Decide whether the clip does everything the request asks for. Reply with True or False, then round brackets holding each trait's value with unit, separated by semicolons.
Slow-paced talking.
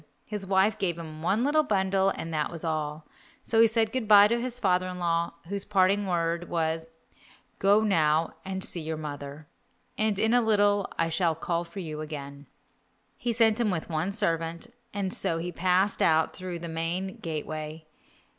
False (185 wpm)